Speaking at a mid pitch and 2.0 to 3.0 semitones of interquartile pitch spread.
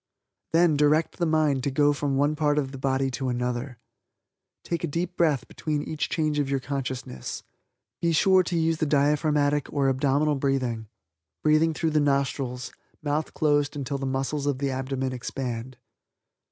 Yes: medium, 145 Hz; narrow, 2.4 semitones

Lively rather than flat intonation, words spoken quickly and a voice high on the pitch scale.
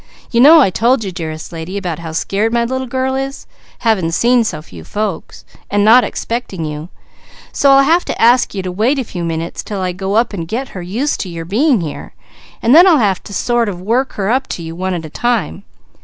Yes: wide, 5.9 semitones; fast, 230 wpm; high, 205 Hz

